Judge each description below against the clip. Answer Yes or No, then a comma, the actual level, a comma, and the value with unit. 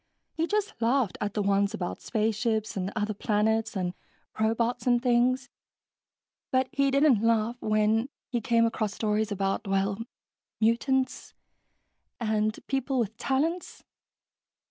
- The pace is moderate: No, slow, 125 wpm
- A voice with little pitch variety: No, average, 3.3 semitones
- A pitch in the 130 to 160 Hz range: No, high, 225 Hz